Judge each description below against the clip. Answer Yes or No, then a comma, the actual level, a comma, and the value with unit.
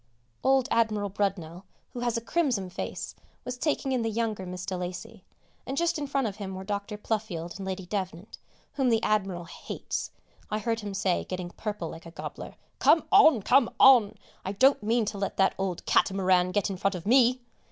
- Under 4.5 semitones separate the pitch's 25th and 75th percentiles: Yes, average, 4.0 semitones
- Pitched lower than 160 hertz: No, high, 205 Hz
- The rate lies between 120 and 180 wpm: No, average, 195 wpm